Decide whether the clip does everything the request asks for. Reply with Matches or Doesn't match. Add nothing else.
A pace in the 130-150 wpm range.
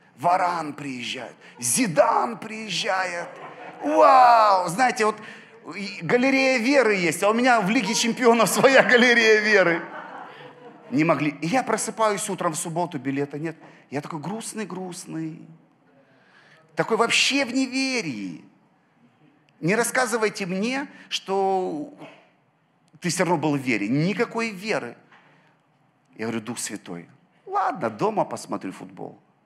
Doesn't match